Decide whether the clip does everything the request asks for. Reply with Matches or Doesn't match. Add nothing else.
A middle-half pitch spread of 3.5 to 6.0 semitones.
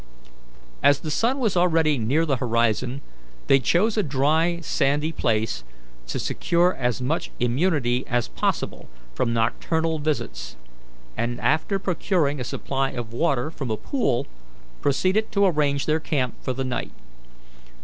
Matches